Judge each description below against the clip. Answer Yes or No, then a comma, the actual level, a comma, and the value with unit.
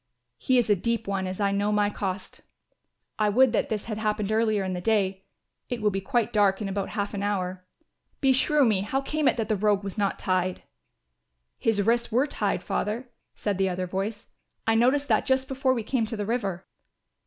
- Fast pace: Yes, fast, 210 wpm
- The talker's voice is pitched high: Yes, high, 210 Hz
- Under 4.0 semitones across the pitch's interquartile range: Yes, average, 3.2 semitones